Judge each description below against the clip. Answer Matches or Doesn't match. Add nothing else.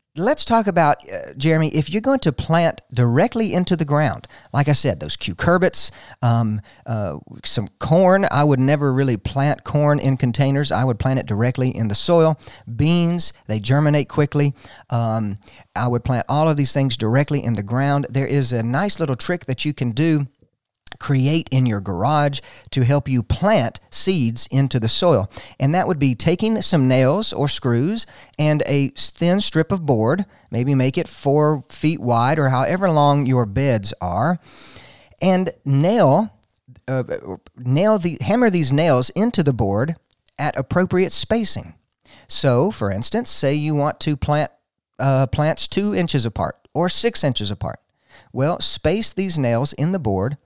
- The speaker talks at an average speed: Matches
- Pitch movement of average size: Matches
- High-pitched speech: Doesn't match